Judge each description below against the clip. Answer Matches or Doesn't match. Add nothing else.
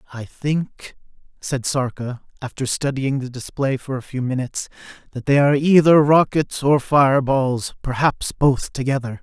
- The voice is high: Doesn't match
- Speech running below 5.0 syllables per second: Matches